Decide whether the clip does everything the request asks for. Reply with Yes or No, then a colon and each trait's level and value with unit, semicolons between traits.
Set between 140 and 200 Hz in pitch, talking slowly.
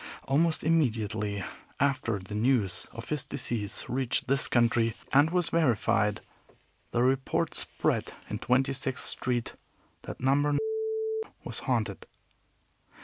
No: low, 125 Hz; slow, 115 wpm